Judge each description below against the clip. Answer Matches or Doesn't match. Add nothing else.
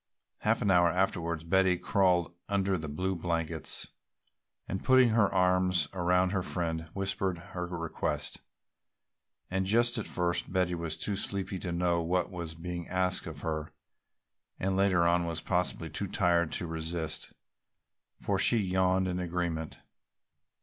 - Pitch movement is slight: Matches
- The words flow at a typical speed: Matches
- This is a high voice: Doesn't match